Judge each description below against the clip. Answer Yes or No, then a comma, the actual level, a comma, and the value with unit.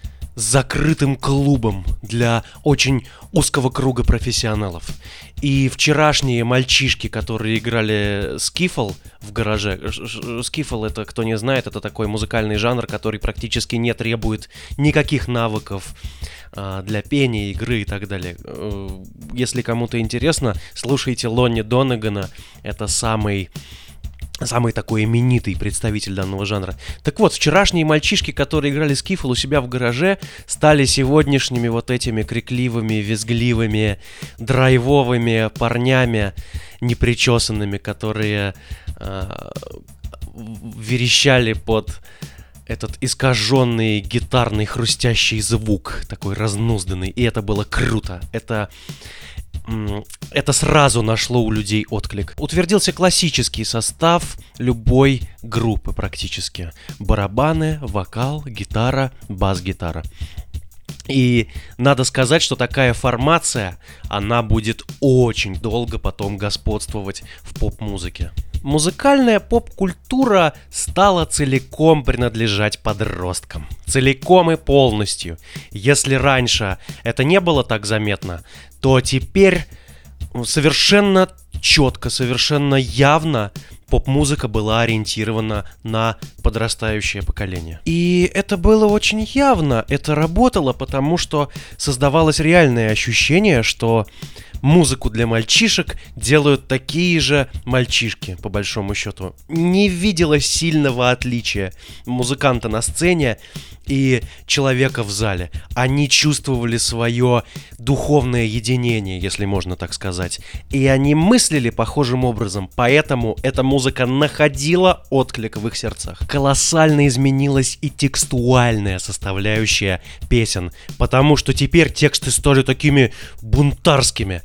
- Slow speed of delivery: Yes, slow, 105 wpm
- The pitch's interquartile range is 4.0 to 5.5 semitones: Yes, average, 5.0 semitones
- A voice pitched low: Yes, low, 115 Hz